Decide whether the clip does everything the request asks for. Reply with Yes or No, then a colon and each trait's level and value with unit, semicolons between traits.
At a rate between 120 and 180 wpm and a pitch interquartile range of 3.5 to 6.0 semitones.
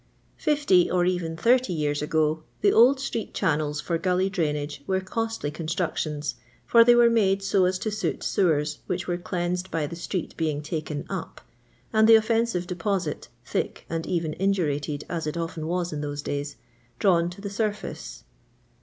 Yes: average, 175 wpm; average, 4.3 semitones